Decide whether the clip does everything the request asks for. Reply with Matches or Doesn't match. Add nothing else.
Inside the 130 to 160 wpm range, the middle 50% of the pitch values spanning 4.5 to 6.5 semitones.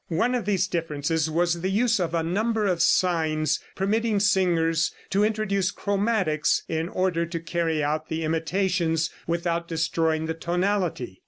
Doesn't match